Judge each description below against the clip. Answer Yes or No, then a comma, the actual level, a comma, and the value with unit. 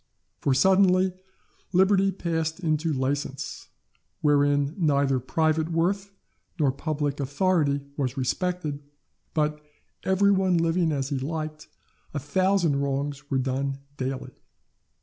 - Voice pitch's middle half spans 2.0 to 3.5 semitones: No, average, 4.3 semitones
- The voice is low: No, medium, 150 Hz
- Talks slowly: Yes, slow, 110 wpm